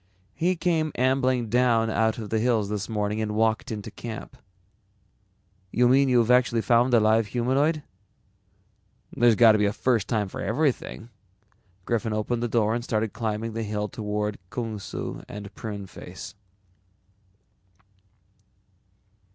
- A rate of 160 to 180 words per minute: No, average, 140 wpm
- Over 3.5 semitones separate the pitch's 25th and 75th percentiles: No, narrow, 2.5 semitones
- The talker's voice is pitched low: Yes, low, 115 Hz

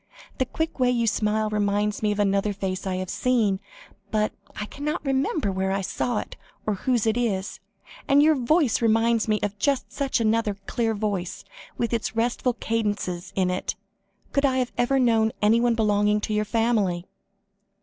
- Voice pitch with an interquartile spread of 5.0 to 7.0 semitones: No, average, 3.0 semitones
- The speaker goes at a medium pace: Yes, average, 170 wpm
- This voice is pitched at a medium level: No, high, 220 Hz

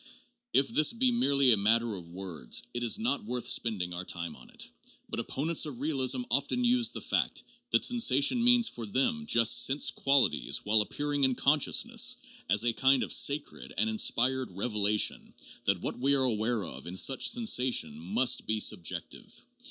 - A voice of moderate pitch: No, low, 130 Hz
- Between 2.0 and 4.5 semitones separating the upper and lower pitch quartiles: No, wide, 5.6 semitones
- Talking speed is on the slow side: No, average, 175 wpm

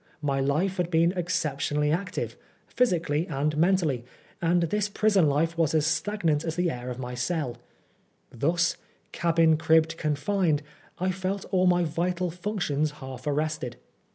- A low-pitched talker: No, medium, 165 Hz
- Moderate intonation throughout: Yes, average, 3.3 semitones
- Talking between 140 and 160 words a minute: Yes, average, 150 wpm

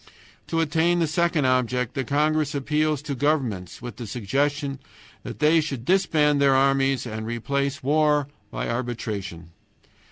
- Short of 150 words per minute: Yes, average, 140 wpm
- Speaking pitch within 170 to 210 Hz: No, medium, 140 Hz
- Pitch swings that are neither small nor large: Yes, average, 3.7 semitones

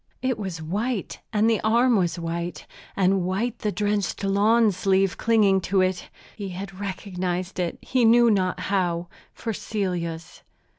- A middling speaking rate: Yes, average, 150 wpm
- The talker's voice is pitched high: Yes, high, 195 Hz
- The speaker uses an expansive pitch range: No, average, 3.2 semitones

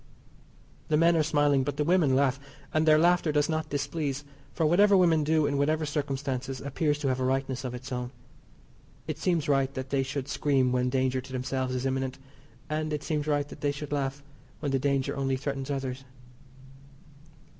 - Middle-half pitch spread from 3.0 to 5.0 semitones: No, narrow, 2.5 semitones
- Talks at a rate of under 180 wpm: No, average, 190 wpm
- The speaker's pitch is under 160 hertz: Yes, medium, 140 Hz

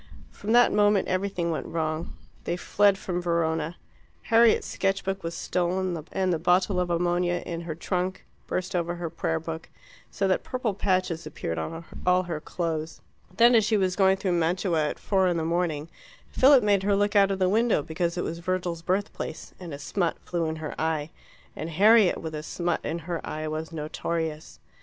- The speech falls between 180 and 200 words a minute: Yes, average, 190 wpm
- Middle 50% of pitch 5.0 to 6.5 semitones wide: No, average, 2.9 semitones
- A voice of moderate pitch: Yes, medium, 175 Hz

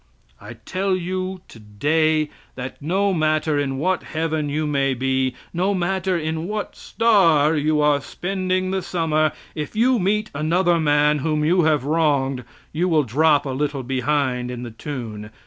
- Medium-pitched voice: Yes, medium, 155 Hz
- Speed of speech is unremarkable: Yes, average, 160 wpm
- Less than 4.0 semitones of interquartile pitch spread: No, average, 4.3 semitones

